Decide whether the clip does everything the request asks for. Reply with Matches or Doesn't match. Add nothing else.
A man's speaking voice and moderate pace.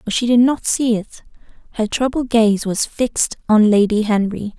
Doesn't match